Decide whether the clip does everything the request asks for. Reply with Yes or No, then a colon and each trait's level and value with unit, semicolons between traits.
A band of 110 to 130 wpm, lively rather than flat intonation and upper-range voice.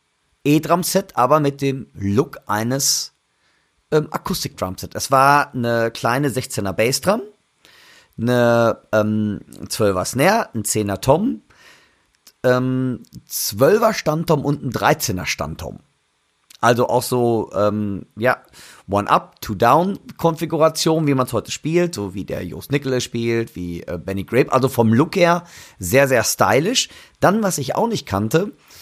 No: slow, 125 wpm; wide, 5.8 semitones; low, 125 Hz